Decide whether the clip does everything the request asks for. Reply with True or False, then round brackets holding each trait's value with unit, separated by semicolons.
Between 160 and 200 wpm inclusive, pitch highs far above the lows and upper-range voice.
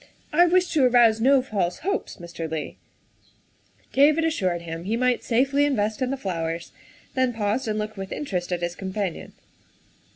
True (165 wpm; 7.1 semitones; 220 Hz)